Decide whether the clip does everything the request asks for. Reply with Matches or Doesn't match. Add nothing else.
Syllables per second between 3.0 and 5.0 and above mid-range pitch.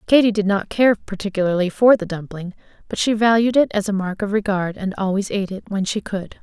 Doesn't match